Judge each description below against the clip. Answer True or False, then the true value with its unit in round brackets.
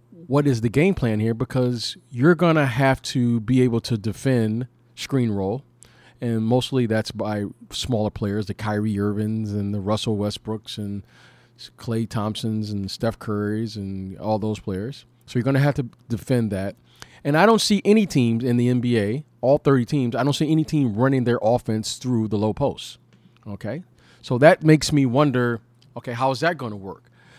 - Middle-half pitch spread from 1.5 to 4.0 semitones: True (3.7 semitones)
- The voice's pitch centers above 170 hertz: False (120 Hz)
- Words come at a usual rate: True (180 wpm)